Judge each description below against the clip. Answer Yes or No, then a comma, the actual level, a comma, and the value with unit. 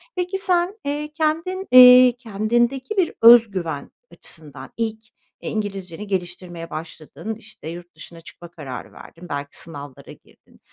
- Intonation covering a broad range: Yes, wide, 7.5 semitones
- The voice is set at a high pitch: Yes, high, 210 Hz